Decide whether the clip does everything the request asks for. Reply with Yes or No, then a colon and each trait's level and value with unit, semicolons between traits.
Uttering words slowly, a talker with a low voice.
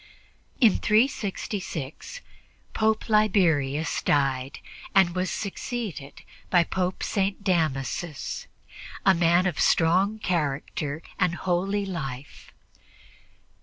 No: slow, 90 wpm; medium, 180 Hz